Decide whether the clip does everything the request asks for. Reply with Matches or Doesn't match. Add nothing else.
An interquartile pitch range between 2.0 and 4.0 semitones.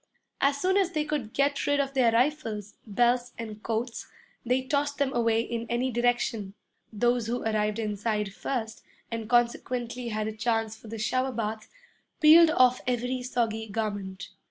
Matches